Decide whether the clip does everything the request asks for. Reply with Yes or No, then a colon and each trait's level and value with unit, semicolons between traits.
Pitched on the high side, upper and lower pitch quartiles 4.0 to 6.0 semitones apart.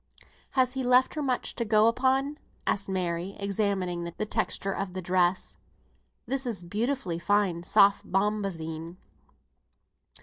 Yes: high, 200 Hz; average, 5.2 semitones